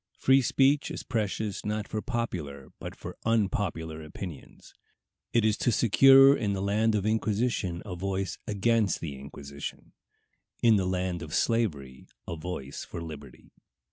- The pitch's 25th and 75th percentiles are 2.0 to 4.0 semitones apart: No, average, 5.3 semitones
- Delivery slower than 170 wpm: Yes, average, 150 wpm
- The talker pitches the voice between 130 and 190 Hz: No, low, 100 Hz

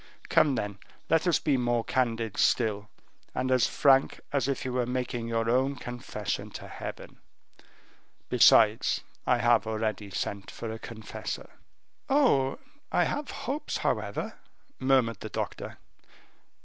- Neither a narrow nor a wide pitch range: Yes, average, 3.0 semitones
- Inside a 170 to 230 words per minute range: No, slow, 135 wpm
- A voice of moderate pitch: No, low, 120 Hz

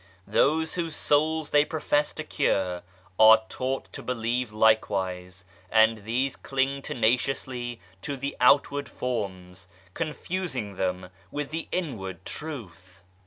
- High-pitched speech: No, low, 125 Hz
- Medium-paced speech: No, slow, 120 wpm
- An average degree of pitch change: No, wide, 6.6 semitones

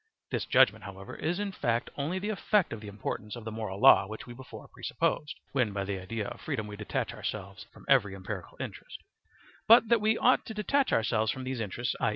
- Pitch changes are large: Yes, wide, 8.7 semitones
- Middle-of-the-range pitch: No, low, 115 Hz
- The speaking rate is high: Yes, fast, 215 wpm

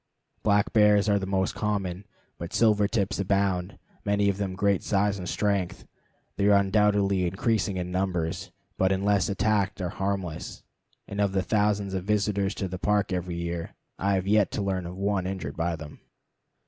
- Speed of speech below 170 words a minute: No, average, 180 wpm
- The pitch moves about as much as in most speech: No, narrow, 1.8 semitones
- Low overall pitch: Yes, low, 100 Hz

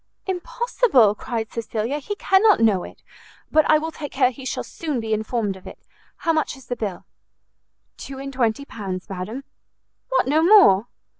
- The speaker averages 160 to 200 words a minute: Yes, average, 170 wpm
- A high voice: Yes, very high, 260 Hz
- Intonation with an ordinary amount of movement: No, wide, 6.2 semitones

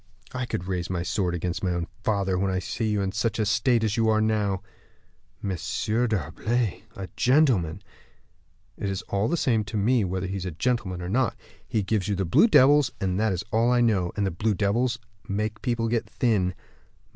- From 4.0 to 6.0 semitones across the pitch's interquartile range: No, average, 3.5 semitones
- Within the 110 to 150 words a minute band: No, average, 195 wpm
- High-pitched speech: No, low, 105 Hz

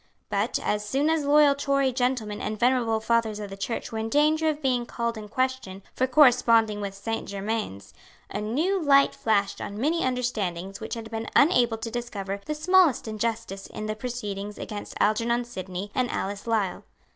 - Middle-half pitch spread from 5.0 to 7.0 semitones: No, average, 3.9 semitones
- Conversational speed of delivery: Yes, average, 180 wpm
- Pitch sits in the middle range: No, high, 230 Hz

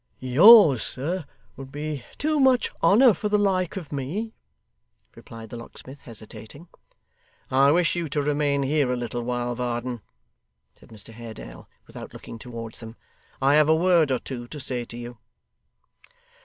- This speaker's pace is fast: No, average, 155 wpm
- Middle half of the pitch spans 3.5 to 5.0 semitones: No, wide, 5.6 semitones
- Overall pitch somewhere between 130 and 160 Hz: Yes, low, 135 Hz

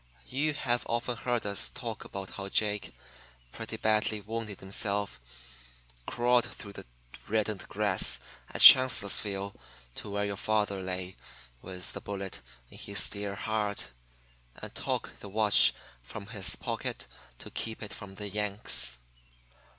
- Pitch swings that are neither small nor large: No, narrow, 2.0 semitones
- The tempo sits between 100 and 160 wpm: Yes, slow, 135 wpm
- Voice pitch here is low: Yes, low, 105 Hz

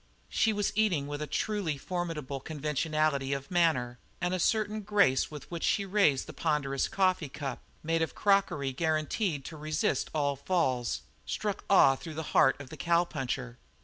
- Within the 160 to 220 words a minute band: Yes, average, 165 wpm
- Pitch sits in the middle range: Yes, medium, 155 Hz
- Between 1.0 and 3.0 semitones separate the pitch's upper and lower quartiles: No, average, 4.8 semitones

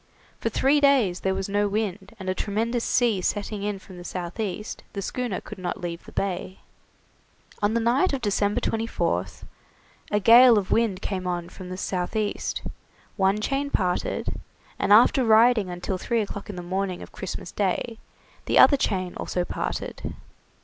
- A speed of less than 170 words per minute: No, average, 175 wpm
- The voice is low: No, high, 200 Hz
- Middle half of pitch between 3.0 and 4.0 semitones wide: Yes, average, 3.5 semitones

